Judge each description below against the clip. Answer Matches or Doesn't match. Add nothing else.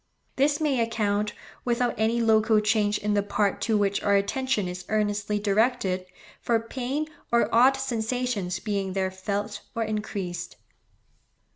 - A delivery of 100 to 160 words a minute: Matches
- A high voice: Matches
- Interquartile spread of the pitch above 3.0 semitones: Doesn't match